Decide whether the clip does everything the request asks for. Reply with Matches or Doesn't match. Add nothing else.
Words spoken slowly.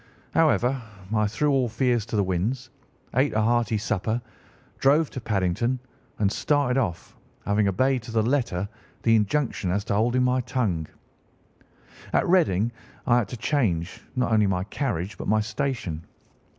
Doesn't match